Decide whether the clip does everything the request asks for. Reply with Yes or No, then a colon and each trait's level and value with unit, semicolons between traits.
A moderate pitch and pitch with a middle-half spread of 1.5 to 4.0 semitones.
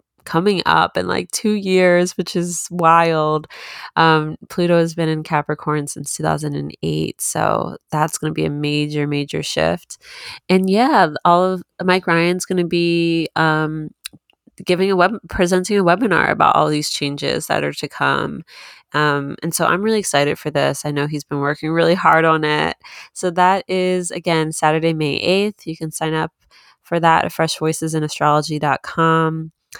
Yes: medium, 160 Hz; average, 3.0 semitones